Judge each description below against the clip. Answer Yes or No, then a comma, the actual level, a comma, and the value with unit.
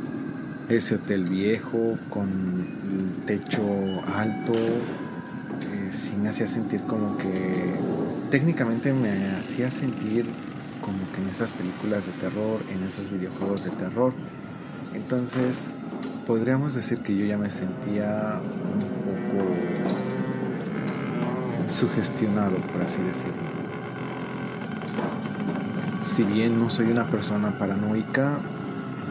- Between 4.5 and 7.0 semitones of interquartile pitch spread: Yes, wide, 5.5 semitones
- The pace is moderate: No, slow, 105 wpm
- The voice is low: Yes, low, 115 Hz